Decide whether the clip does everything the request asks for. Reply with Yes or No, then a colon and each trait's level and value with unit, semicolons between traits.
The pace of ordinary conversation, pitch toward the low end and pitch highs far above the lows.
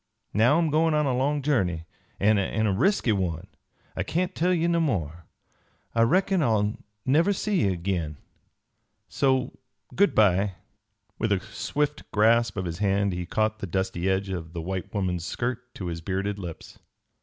Yes: average, 165 wpm; low, 105 Hz; wide, 7.3 semitones